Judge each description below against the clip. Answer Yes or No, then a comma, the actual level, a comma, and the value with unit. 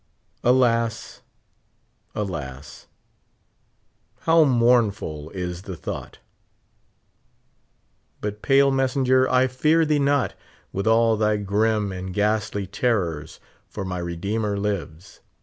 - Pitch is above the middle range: No, low, 105 Hz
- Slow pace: Yes, slow, 95 wpm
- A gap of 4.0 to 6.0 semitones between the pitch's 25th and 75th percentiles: Yes, average, 5.1 semitones